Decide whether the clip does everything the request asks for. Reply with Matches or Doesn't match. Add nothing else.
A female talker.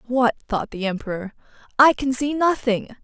Matches